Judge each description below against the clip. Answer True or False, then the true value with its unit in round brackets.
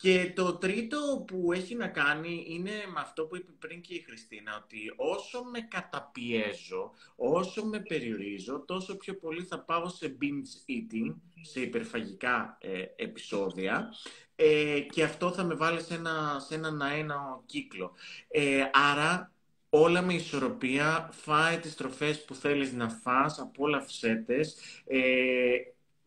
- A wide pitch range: False (4.9 semitones)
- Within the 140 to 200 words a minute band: True (145 wpm)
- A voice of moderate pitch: True (160 Hz)